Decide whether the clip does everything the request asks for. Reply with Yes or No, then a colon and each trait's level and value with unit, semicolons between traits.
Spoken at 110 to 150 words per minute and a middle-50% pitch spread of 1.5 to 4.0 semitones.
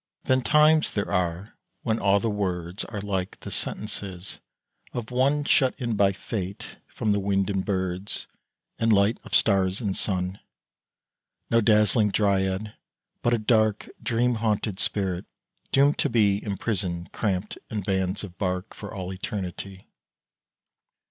Yes: average, 140 wpm; average, 2.7 semitones